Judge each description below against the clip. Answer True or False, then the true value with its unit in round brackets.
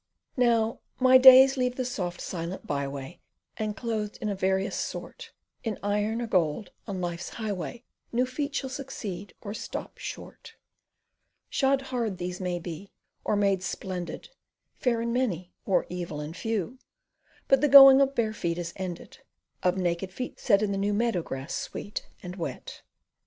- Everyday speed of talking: True (160 wpm)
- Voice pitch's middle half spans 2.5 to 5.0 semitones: False (5.5 semitones)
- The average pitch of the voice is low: False (205 Hz)